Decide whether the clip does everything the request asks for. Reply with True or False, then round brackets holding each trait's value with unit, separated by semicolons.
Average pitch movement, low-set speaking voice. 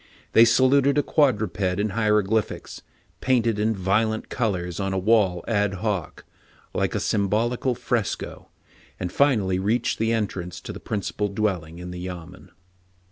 True (3.4 semitones; 105 Hz)